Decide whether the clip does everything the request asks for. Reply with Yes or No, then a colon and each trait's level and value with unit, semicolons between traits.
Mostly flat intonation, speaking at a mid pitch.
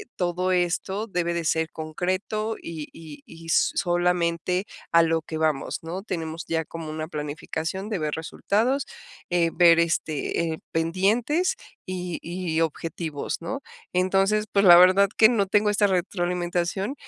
No: average, 3.0 semitones; medium, 175 Hz